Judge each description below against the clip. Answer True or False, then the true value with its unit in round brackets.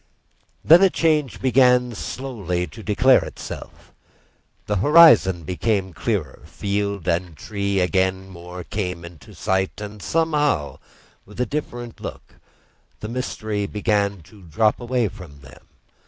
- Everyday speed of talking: False (125 wpm)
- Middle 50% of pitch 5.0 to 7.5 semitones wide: True (5.3 semitones)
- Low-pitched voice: True (105 Hz)